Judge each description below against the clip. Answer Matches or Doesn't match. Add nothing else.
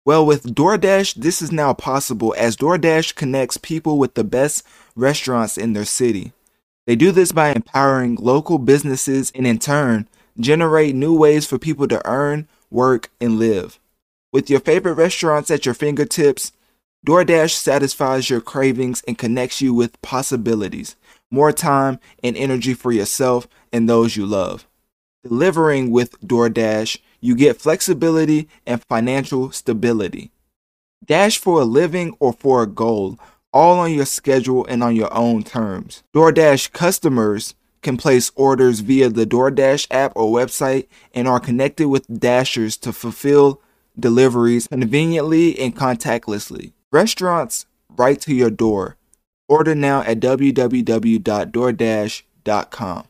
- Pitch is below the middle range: Matches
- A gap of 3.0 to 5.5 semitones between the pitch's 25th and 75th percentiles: Matches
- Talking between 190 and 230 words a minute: Doesn't match